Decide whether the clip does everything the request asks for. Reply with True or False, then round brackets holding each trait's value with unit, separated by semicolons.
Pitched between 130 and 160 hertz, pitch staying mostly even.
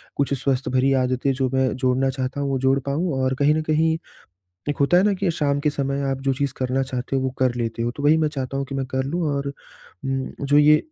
True (135 Hz; 1.7 semitones)